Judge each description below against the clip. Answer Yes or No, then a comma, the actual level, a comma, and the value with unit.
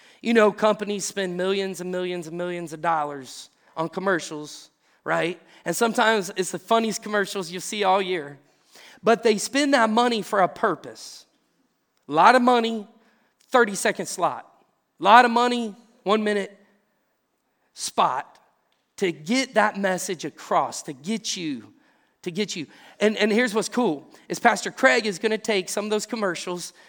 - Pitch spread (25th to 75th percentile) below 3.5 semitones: No, average, 4.1 semitones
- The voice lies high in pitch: Yes, high, 205 Hz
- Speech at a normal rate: Yes, average, 165 wpm